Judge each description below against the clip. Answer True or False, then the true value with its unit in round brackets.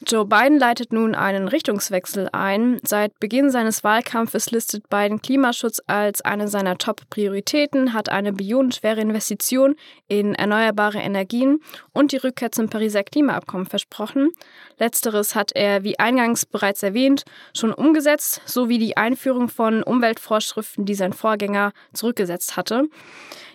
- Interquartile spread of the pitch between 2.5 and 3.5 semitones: False (4.1 semitones)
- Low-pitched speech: False (220 Hz)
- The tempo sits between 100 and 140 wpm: True (130 wpm)